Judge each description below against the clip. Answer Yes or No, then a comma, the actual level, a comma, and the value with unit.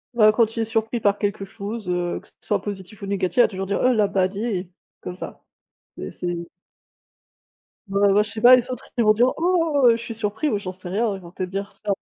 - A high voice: Yes, high, 205 Hz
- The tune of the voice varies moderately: Yes, average, 3.0 semitones